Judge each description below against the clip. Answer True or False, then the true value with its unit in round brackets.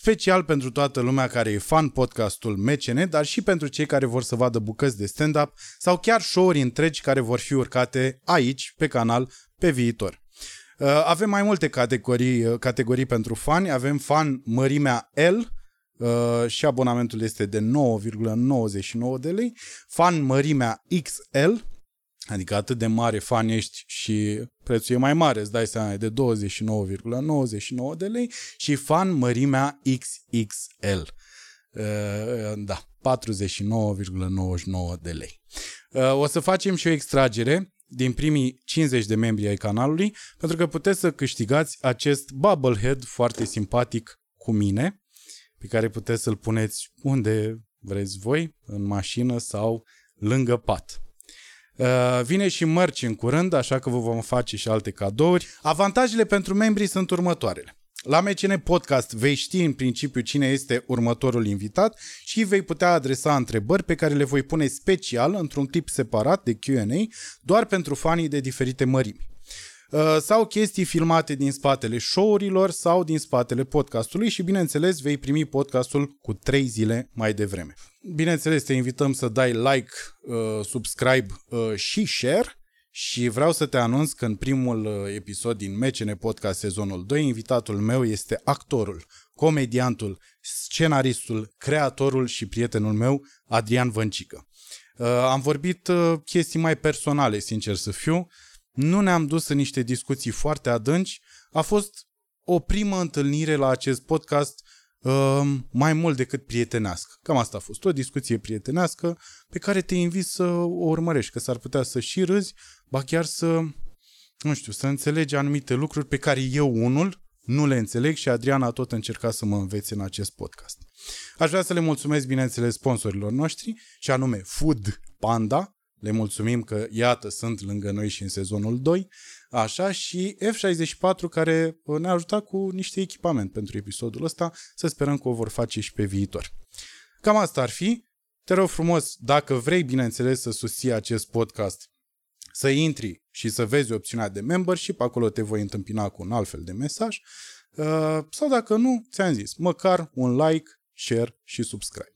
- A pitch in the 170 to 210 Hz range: False (130 Hz)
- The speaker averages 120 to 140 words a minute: False (155 wpm)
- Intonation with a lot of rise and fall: True (6.1 semitones)